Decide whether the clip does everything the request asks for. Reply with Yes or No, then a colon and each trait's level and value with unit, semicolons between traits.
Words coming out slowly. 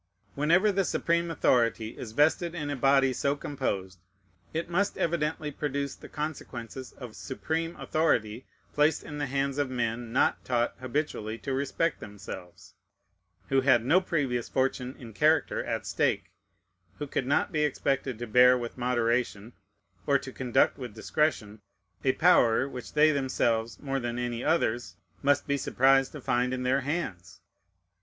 No: average, 155 wpm